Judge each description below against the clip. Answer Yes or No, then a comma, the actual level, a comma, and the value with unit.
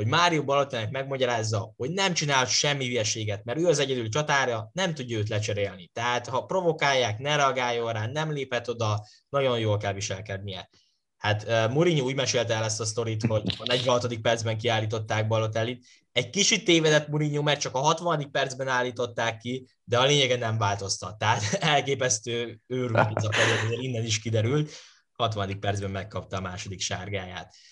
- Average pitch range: Yes, average, 4.0 semitones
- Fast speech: Yes, fast, 160 wpm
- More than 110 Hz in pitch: Yes, low, 120 Hz